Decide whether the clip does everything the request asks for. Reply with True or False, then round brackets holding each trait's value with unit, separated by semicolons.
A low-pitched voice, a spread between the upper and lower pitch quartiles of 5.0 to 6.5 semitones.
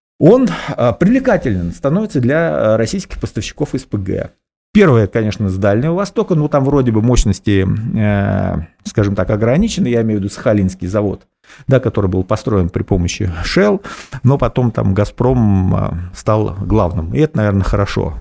True (110 Hz; 5.4 semitones)